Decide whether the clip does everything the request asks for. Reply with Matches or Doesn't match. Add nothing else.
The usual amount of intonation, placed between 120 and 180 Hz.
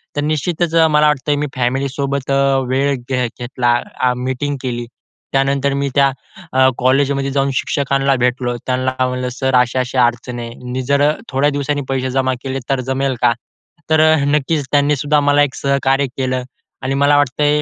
Doesn't match